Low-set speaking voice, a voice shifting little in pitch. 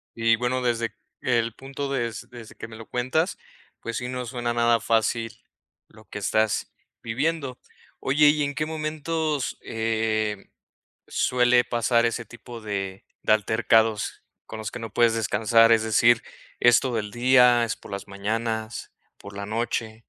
Yes: low, 115 Hz; narrow, 2.1 semitones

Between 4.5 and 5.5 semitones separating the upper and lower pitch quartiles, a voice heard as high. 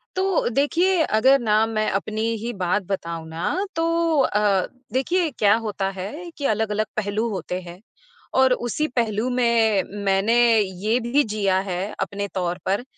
Yes: average, 5.1 semitones; high, 215 Hz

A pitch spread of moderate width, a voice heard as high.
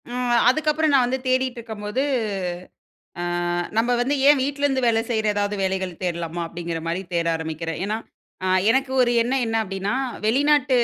No: wide, 5.7 semitones; high, 230 Hz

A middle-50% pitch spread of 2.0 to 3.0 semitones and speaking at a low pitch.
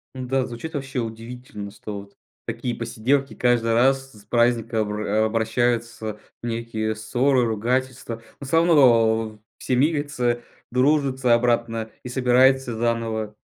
Yes: narrow, 2.6 semitones; low, 120 Hz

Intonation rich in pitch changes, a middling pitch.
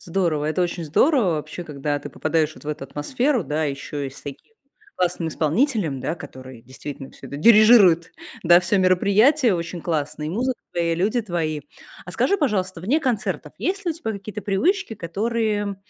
Yes: wide, 6.3 semitones; medium, 180 Hz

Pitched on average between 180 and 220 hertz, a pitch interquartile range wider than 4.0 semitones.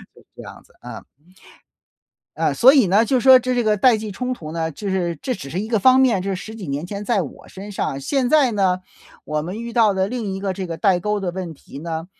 Yes: high, 200 Hz; average, 4.9 semitones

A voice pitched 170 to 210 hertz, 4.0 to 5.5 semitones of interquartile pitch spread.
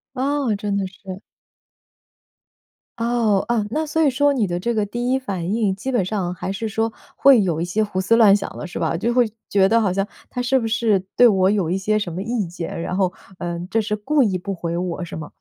Yes: high, 205 Hz; average, 4.3 semitones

